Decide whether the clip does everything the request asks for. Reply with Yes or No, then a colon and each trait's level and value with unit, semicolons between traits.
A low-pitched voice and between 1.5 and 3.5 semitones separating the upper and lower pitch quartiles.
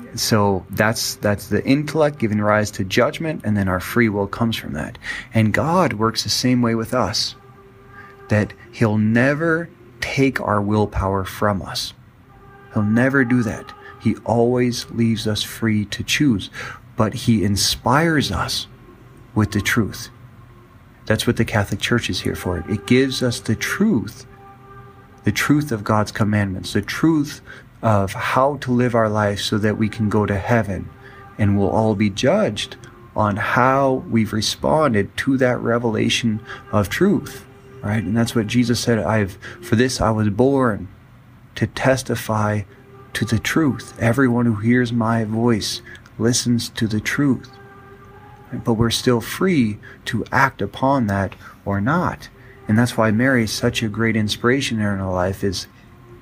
Yes: low, 115 Hz; average, 3.2 semitones